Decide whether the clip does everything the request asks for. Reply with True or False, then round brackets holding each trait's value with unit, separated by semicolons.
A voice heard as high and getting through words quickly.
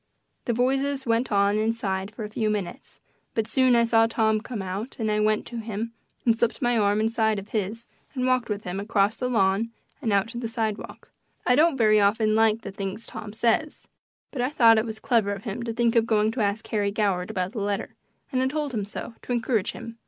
True (220 Hz; 225 wpm)